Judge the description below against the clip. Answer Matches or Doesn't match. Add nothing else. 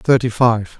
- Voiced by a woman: Doesn't match